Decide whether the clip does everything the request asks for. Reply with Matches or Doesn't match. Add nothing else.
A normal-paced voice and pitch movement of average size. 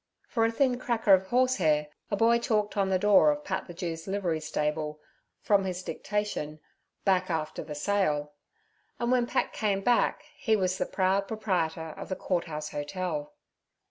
Matches